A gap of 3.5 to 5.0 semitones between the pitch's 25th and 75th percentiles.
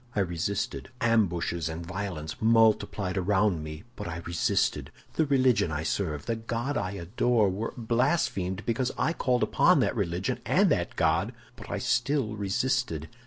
No: wide, 5.4 semitones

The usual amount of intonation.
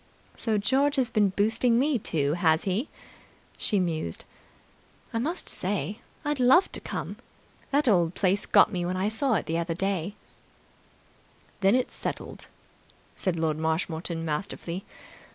No: wide, 5.7 semitones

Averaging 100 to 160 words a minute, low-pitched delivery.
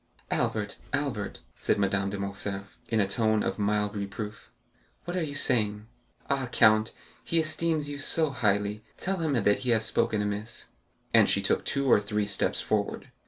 No: average, 170 wpm; low, 110 Hz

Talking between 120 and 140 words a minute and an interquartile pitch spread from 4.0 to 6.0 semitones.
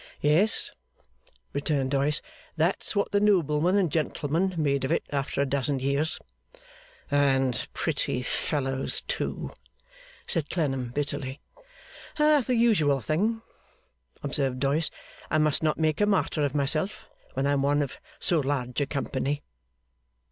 No: slow, 135 wpm; average, 3.2 semitones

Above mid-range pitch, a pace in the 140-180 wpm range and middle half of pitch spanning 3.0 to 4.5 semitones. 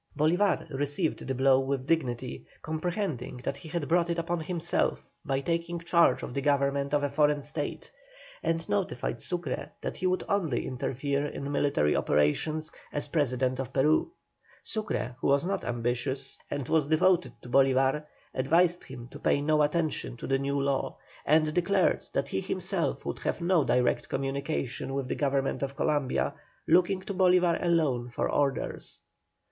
No: medium, 145 Hz; average, 165 wpm; average, 3.9 semitones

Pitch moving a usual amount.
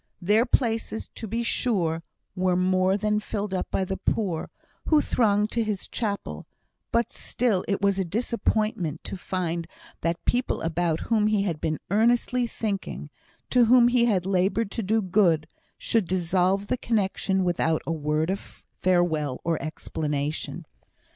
Yes: average, 4.3 semitones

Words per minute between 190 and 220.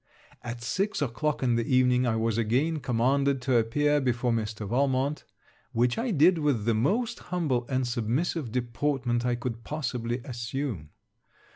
No: average, 150 wpm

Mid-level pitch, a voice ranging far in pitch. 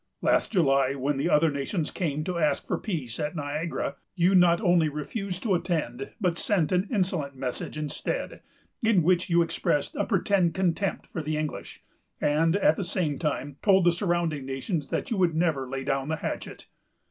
No: medium, 165 Hz; average, 3.9 semitones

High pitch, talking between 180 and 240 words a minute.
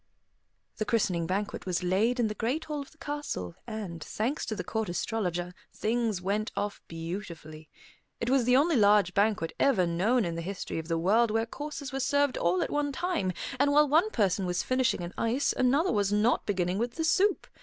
Yes: high, 215 Hz; average, 200 wpm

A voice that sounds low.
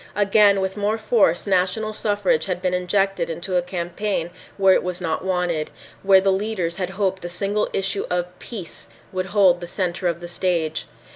No: medium, 185 Hz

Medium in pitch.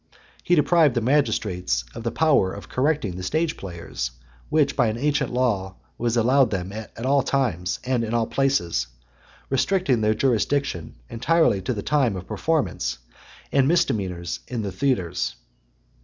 No: low, 120 Hz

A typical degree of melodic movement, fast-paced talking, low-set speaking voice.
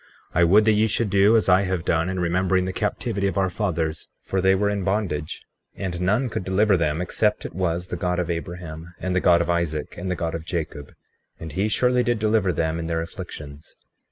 Yes: average, 3.2 semitones; fast, 230 wpm; very low, 90 Hz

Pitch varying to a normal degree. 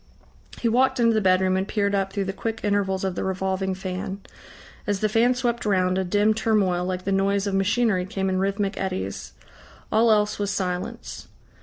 No: narrow, 2.2 semitones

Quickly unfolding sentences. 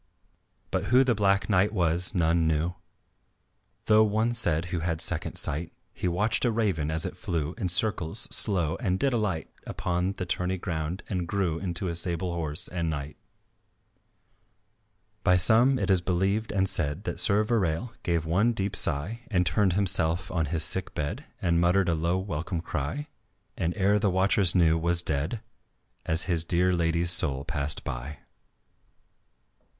No: average, 165 wpm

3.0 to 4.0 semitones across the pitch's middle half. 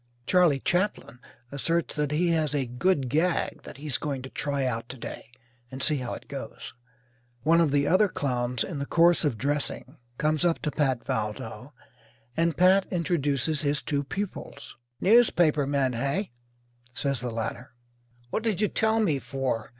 No: average, 4.5 semitones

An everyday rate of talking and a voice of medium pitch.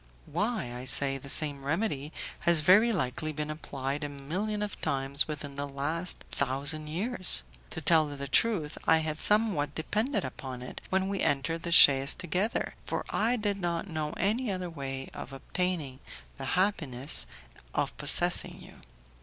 Yes: average, 160 wpm; medium, 155 Hz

